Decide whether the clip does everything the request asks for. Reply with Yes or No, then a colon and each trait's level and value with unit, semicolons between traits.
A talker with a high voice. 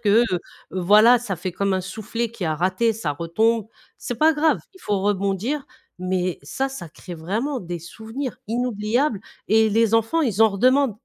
Yes: high, 215 Hz